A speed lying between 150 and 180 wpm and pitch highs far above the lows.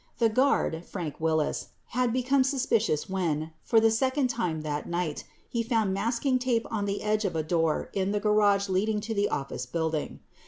No: average, 190 wpm; wide, 6.0 semitones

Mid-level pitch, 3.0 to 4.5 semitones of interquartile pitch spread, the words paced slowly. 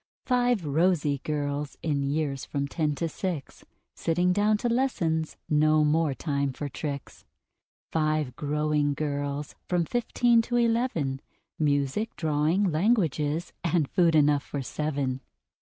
Yes: medium, 155 Hz; average, 3.7 semitones; slow, 125 wpm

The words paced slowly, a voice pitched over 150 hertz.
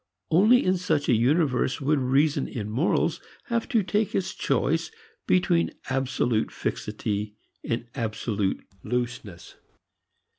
No: slow, 115 wpm; low, 135 Hz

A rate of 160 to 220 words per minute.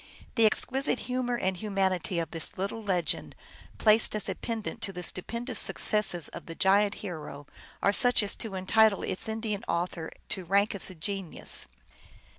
Yes: average, 165 wpm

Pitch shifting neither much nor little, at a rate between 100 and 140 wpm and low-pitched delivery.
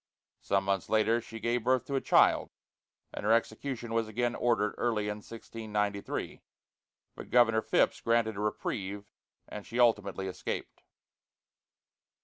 No: narrow, 2.2 semitones; slow, 135 wpm; low, 110 Hz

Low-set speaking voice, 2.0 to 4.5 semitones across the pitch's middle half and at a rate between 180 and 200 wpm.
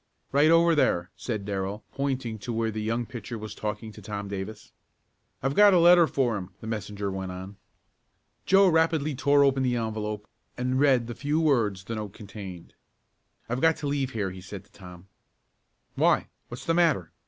No: low, 115 Hz; wide, 5.6 semitones; average, 185 wpm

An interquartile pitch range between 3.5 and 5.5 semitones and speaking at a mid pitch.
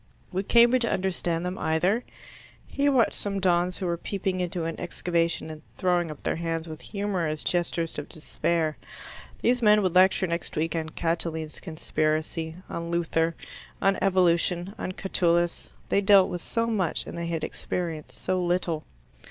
No: narrow, 2.6 semitones; medium, 175 Hz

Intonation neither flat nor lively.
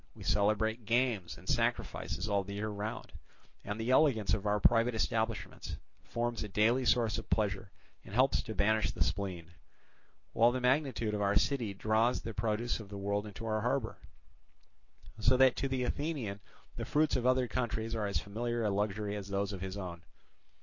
Yes: average, 3.0 semitones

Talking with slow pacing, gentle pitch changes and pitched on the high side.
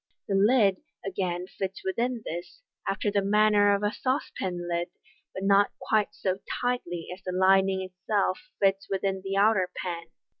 No: average, 155 wpm; narrow, 1.8 semitones; high, 195 Hz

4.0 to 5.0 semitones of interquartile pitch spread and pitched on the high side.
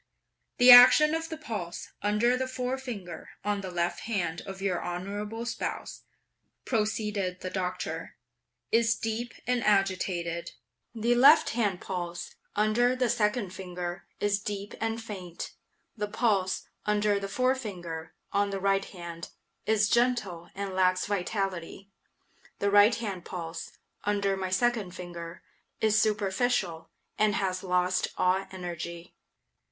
No: average, 3.6 semitones; high, 200 Hz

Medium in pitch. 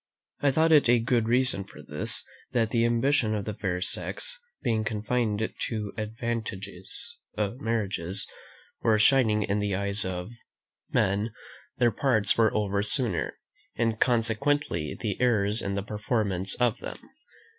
No: low, 110 Hz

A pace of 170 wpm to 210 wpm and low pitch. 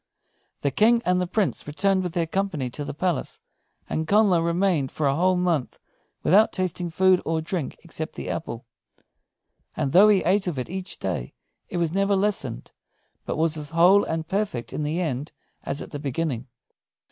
No: average, 180 wpm; medium, 170 Hz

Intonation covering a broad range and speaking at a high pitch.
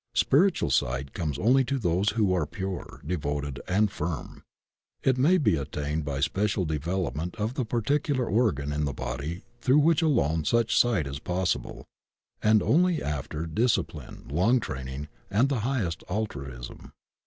No: wide, 8.4 semitones; very low, 90 Hz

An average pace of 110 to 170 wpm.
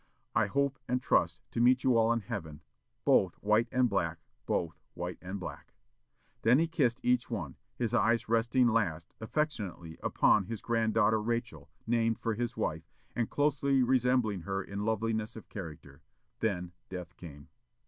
Yes: average, 160 wpm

